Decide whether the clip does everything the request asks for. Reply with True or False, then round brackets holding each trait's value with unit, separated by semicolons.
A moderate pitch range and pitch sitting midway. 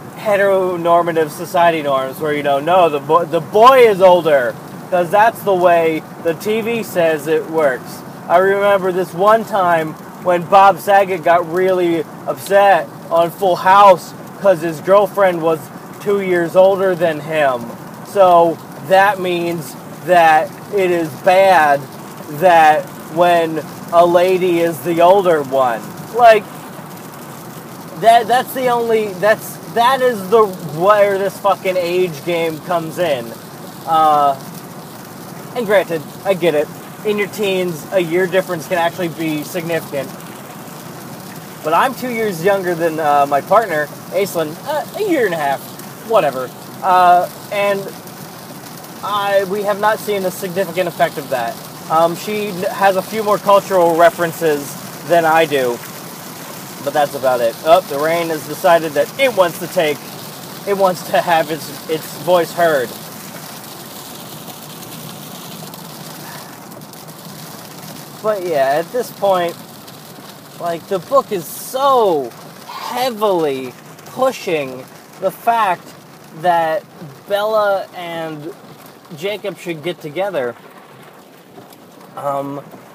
True (3.0 semitones; 180 Hz)